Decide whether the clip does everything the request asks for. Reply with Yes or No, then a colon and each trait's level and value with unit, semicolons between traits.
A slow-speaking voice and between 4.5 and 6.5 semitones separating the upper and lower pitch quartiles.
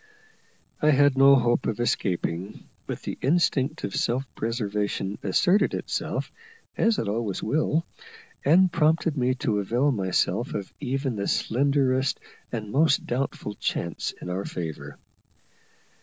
Yes: slow, 130 wpm; wide, 5.6 semitones